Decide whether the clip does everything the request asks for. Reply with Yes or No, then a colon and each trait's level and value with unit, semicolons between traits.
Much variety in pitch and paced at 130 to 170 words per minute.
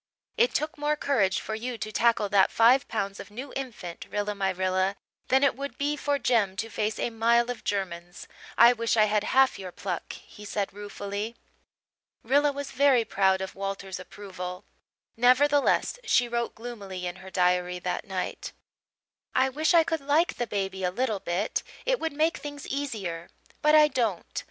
No: wide, 6.1 semitones; average, 180 wpm